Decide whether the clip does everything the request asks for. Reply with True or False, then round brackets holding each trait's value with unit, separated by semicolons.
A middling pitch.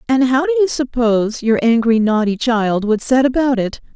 False (240 Hz)